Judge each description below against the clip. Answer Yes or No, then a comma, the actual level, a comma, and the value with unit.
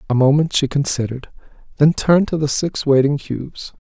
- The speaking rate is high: No, average, 170 wpm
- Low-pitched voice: No, medium, 145 Hz